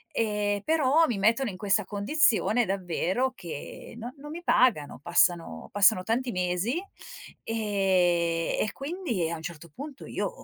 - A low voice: No, high, 205 Hz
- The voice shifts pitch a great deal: Yes, wide, 6.0 semitones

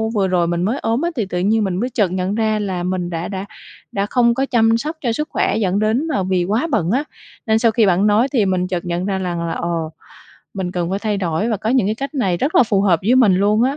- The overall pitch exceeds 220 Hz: No, high, 205 Hz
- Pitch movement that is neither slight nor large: Yes, average, 4.0 semitones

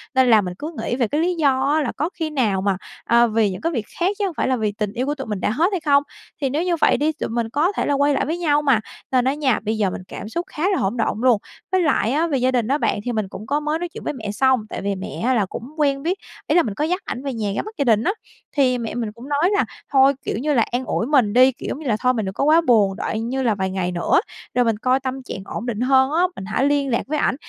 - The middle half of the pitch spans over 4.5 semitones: Yes, average, 5.1 semitones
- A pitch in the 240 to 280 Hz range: Yes, very high, 260 Hz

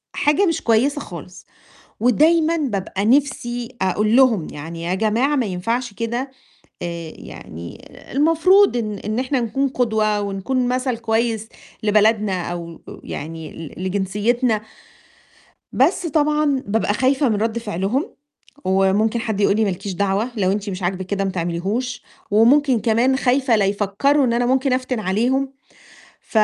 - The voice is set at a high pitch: Yes, high, 225 Hz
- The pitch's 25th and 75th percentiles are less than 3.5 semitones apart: No, average, 4.8 semitones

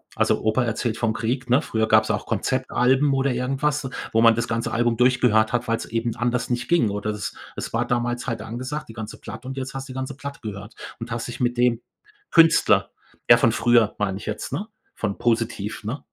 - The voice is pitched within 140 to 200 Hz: No, low, 120 Hz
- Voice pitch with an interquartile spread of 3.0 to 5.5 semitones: No, narrow, 2.5 semitones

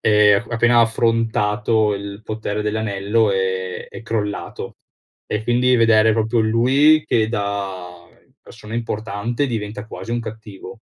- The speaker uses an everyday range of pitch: No, narrow, 2.1 semitones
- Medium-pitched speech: No, low, 110 Hz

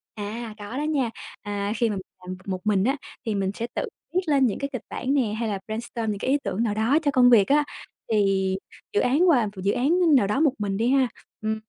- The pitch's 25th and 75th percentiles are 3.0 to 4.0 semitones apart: No, average, 4.7 semitones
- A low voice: No, high, 225 Hz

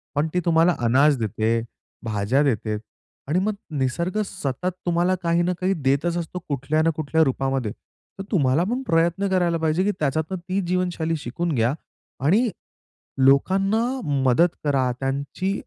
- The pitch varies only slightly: No, average, 5.1 semitones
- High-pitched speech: No, medium, 160 Hz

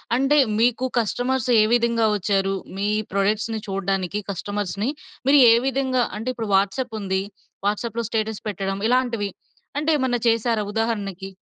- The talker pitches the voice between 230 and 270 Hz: No, high, 220 Hz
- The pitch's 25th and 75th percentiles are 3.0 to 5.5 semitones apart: Yes, average, 3.6 semitones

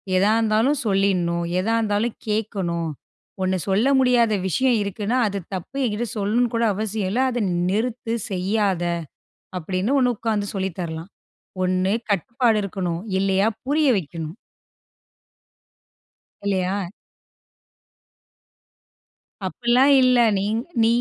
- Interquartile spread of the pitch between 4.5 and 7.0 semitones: No, average, 3.8 semitones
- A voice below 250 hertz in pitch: Yes, high, 205 Hz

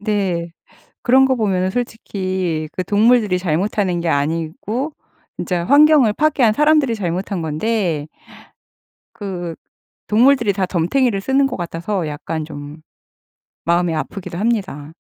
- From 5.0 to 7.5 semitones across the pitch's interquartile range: Yes, wide, 5.4 semitones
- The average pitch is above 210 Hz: No, high, 190 Hz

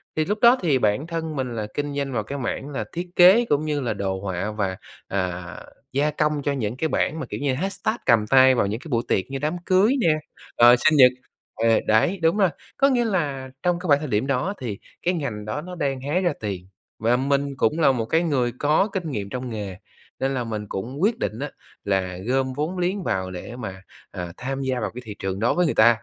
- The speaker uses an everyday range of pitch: No, wide, 6.4 semitones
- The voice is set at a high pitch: No, low, 135 Hz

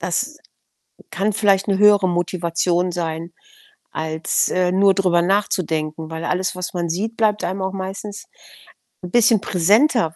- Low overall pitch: No, medium, 185 Hz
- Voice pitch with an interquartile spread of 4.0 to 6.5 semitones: No, average, 2.8 semitones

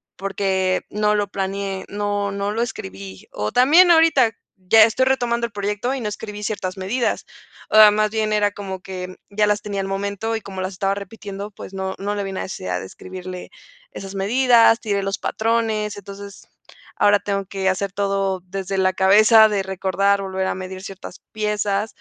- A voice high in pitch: Yes, high, 200 Hz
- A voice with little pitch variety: Yes, narrow, 1.9 semitones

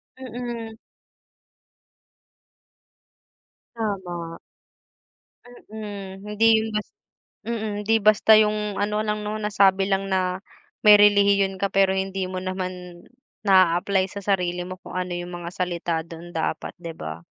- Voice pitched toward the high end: Yes, high, 195 Hz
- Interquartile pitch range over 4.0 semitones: No, narrow, 2.6 semitones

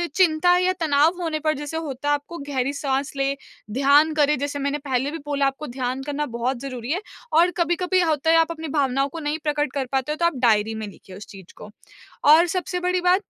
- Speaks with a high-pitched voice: Yes, very high, 290 Hz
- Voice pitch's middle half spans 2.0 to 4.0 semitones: Yes, average, 3.3 semitones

